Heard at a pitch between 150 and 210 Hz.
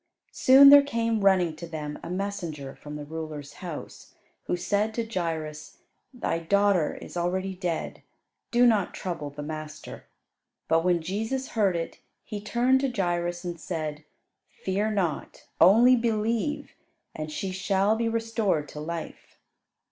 Yes: medium, 185 Hz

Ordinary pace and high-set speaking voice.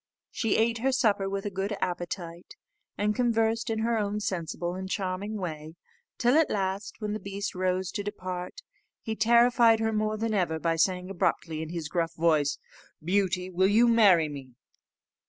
Yes: average, 175 wpm; high, 195 Hz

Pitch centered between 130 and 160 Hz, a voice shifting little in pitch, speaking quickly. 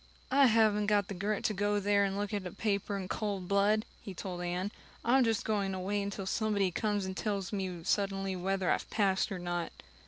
No: high, 200 Hz; narrow, 1.6 semitones; fast, 215 wpm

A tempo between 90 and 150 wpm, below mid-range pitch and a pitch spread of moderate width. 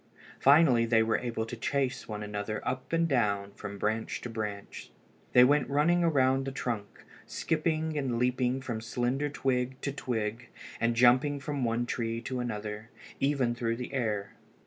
No: average, 165 wpm; low, 125 Hz; average, 3.3 semitones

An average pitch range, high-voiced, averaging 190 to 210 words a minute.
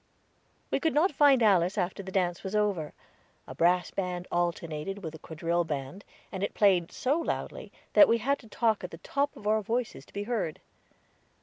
Yes: average, 4.6 semitones; high, 195 Hz; average, 195 wpm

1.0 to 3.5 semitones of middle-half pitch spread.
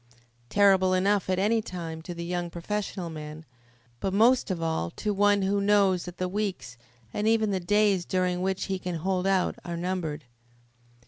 Yes: narrow, 2.6 semitones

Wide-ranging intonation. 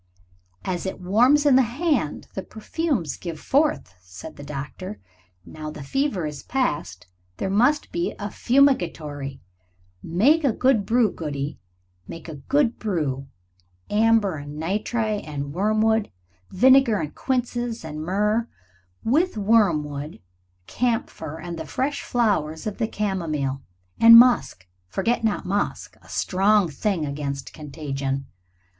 Yes: wide, 7.7 semitones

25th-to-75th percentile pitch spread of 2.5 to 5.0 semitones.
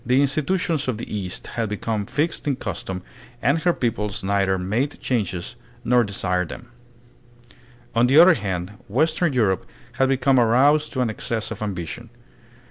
No: wide, 5.6 semitones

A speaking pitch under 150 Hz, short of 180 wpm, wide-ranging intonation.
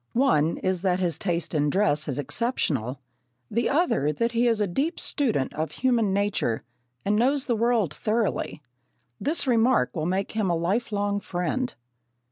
No: high, 205 Hz; average, 160 wpm; wide, 6.1 semitones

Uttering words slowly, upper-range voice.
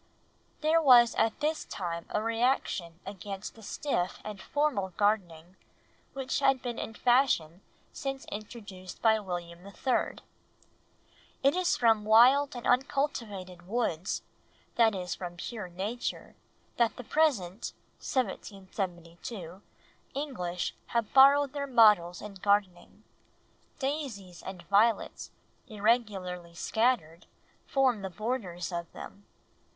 Yes: slow, 115 wpm; high, 210 Hz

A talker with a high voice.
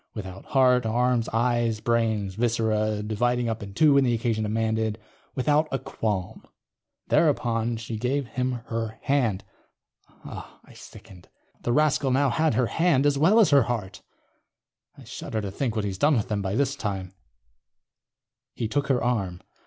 No: low, 115 Hz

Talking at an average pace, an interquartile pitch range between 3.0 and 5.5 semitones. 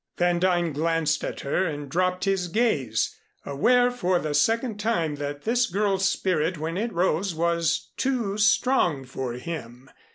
Yes: average, 155 wpm; average, 5.2 semitones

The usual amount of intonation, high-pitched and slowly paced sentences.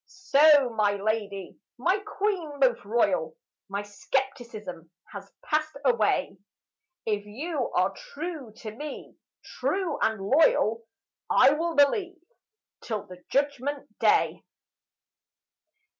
No: wide, 6.8 semitones; high, 245 Hz; slow, 105 wpm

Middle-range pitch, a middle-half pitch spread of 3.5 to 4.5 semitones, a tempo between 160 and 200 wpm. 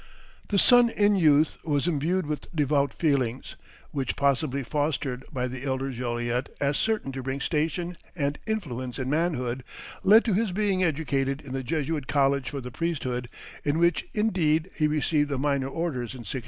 Yes: medium, 145 Hz; average, 4.1 semitones; average, 170 wpm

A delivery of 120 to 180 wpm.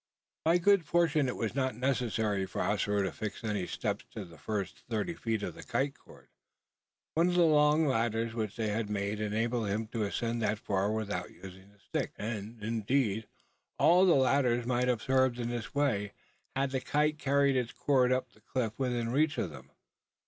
No: average, 195 wpm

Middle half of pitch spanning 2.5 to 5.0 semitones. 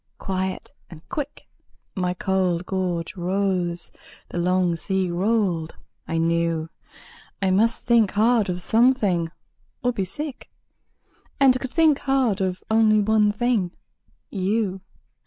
Yes: average, 4.1 semitones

